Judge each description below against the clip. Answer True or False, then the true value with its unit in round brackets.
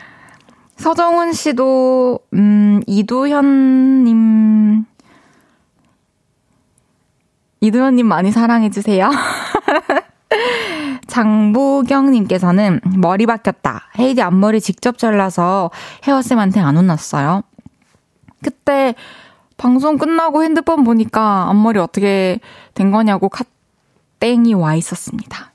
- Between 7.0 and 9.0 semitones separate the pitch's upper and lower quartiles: False (5.1 semitones)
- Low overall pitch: False (230 Hz)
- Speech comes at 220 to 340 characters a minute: False (205 characters per minute)